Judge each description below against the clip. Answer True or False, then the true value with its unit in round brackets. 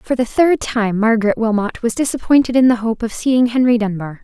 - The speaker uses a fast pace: True (215 wpm)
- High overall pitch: True (230 Hz)